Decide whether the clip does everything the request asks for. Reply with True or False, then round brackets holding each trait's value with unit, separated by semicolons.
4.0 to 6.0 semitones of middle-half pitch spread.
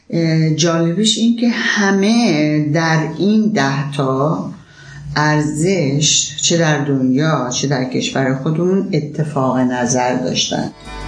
False (3.5 semitones)